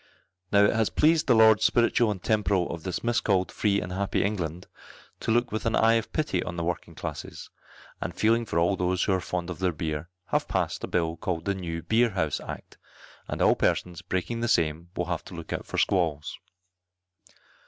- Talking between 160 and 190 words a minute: No, fast, 205 wpm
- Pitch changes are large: No, average, 4.4 semitones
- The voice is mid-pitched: No, very low, 95 Hz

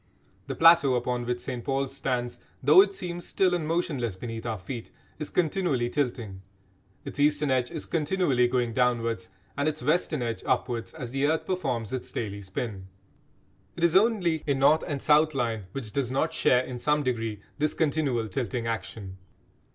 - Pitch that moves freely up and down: No, average, 4.6 semitones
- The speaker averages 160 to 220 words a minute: Yes, average, 175 wpm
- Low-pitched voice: Yes, low, 130 Hz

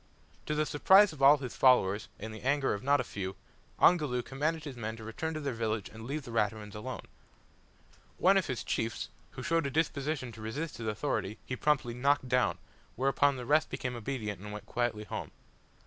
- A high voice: No, low, 130 Hz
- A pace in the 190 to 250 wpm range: Yes, average, 200 wpm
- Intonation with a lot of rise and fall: No, average, 4.8 semitones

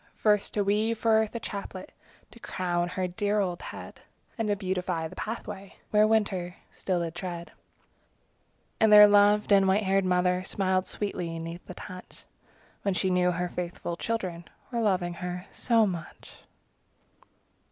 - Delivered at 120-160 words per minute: Yes, average, 155 wpm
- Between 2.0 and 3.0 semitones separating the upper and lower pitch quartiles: Yes, average, 2.7 semitones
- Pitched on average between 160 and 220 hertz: Yes, high, 190 Hz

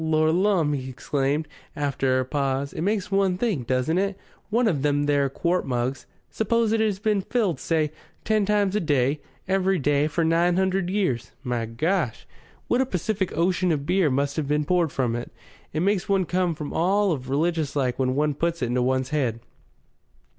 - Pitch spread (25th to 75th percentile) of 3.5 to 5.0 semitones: No, wide, 5.5 semitones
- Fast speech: No, average, 190 wpm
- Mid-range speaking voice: Yes, medium, 160 Hz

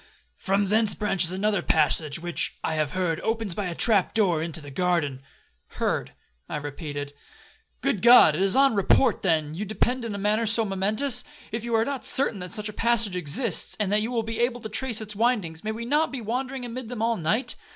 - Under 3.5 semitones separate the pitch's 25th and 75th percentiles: No, average, 5.0 semitones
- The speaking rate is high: Yes, fast, 210 wpm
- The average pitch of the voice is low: No, high, 210 Hz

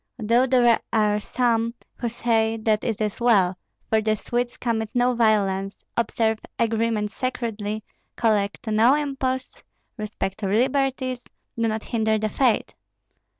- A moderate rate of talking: No, slow, 130 wpm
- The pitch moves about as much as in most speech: No, narrow, 2.2 semitones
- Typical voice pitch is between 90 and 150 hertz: No, high, 225 Hz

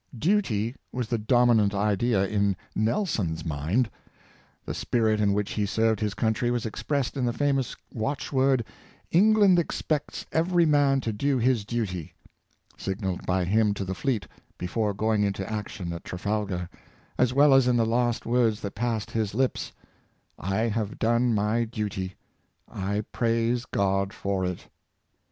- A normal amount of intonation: Yes, average, 3.7 semitones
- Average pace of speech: Yes, average, 160 wpm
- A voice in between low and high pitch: No, low, 110 Hz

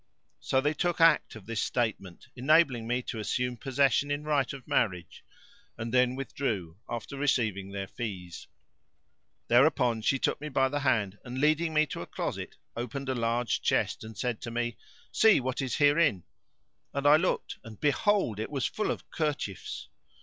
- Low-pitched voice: Yes, low, 125 Hz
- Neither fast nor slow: Yes, average, 170 wpm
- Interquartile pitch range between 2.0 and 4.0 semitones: No, average, 4.4 semitones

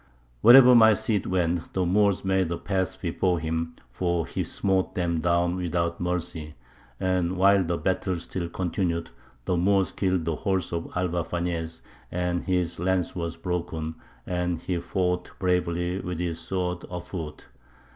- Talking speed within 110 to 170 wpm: Yes, average, 150 wpm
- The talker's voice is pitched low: Yes, very low, 90 Hz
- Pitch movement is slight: Yes, narrow, 1.7 semitones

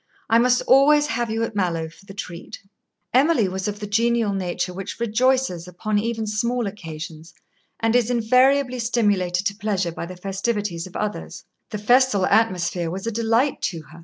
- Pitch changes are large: No, average, 4.4 semitones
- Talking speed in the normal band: Yes, average, 175 wpm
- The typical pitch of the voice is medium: No, high, 210 Hz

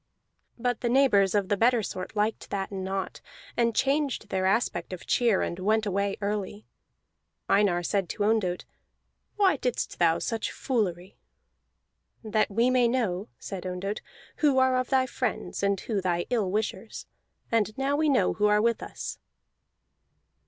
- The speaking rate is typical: Yes, average, 155 wpm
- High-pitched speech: Yes, high, 210 Hz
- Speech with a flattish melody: No, average, 4.0 semitones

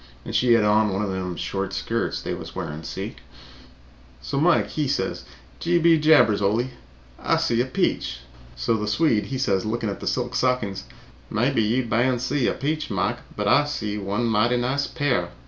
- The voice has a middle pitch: No, low, 115 Hz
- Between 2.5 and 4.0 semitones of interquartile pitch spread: No, average, 4.4 semitones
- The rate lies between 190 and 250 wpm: Yes, average, 195 wpm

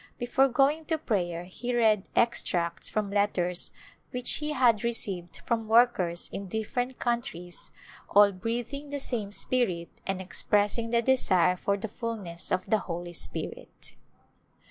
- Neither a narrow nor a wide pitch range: Yes, average, 4.8 semitones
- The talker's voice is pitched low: No, high, 215 Hz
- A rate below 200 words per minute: Yes, average, 145 wpm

